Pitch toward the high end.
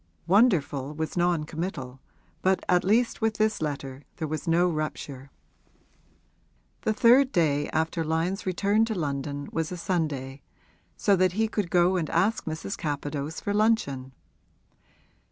No: medium, 165 Hz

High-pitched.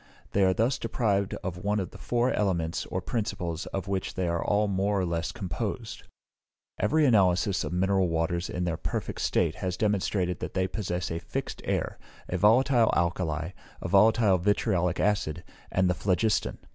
No: very low, 95 Hz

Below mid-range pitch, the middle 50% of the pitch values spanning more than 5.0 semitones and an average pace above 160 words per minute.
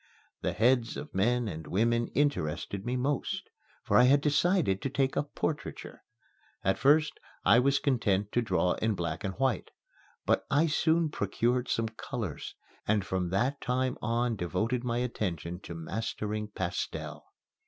No: low, 115 Hz; wide, 5.6 semitones; average, 155 wpm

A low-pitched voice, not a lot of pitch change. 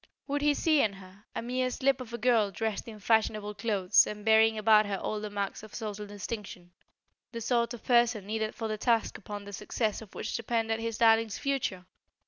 No: high, 220 Hz; narrow, 2.2 semitones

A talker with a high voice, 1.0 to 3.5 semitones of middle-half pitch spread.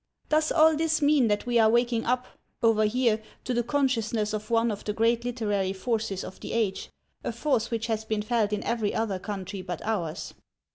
Yes: high, 225 Hz; narrow, 2.5 semitones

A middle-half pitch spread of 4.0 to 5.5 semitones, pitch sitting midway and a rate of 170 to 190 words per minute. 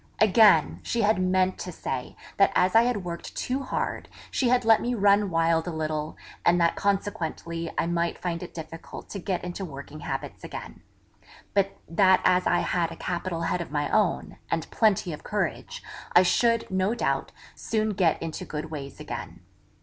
No: average, 3.5 semitones; medium, 180 Hz; average, 180 wpm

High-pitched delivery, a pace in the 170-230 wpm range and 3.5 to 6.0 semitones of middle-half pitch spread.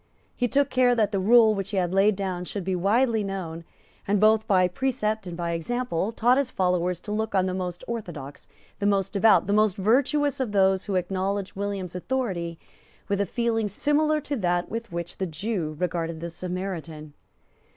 Yes: high, 195 Hz; average, 190 wpm; average, 3.9 semitones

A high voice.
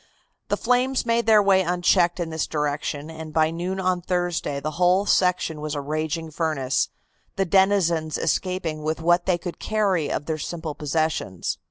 No: medium, 170 Hz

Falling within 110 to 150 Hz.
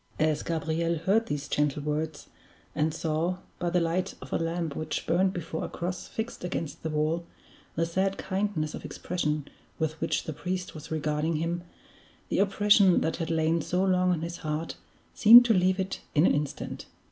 No: medium, 165 Hz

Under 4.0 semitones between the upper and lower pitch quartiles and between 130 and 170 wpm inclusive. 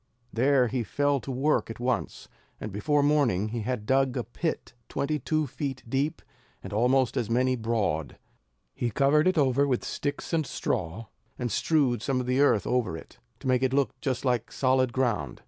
No: average, 3.2 semitones; average, 185 wpm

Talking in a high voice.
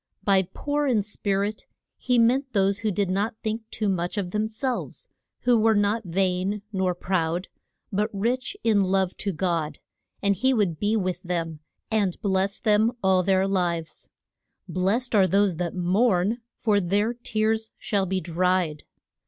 Yes: high, 200 Hz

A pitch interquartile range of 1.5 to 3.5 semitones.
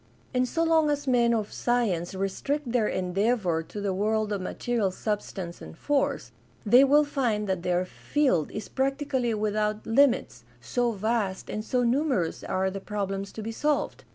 No: average, 4.7 semitones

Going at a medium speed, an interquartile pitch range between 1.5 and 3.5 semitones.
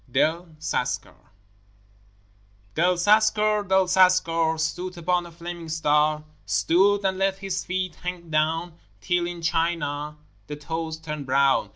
No: slow, 130 wpm; average, 2.8 semitones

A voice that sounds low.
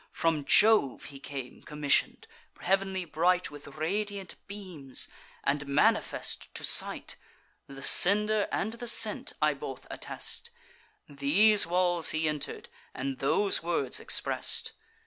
No: medium, 170 Hz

